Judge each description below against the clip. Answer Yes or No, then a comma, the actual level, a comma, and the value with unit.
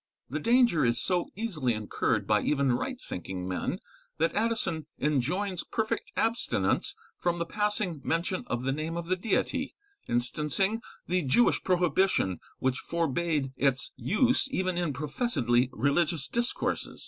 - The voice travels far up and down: Yes, wide, 7.0 semitones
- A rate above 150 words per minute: No, slow, 135 wpm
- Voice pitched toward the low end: No, medium, 170 Hz